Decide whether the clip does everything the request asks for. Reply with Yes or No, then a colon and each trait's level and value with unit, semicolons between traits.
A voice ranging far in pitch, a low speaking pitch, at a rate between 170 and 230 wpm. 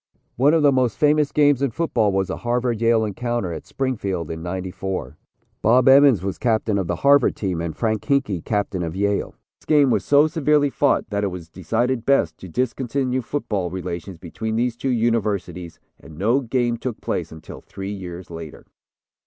Yes: wide, 5.9 semitones; low, 110 Hz; average, 185 wpm